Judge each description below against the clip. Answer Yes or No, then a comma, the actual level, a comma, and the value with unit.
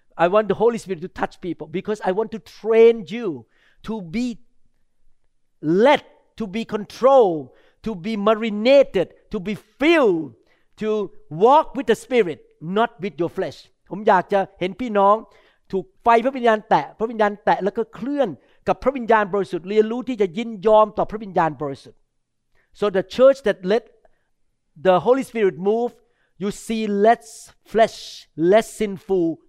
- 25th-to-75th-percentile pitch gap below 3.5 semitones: Yes, average, 2.8 semitones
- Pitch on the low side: No, high, 215 Hz